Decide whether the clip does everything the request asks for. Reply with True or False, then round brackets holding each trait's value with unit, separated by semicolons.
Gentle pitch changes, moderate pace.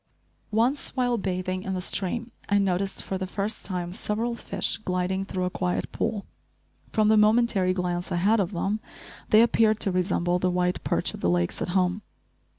False (3.0 semitones; 185 wpm)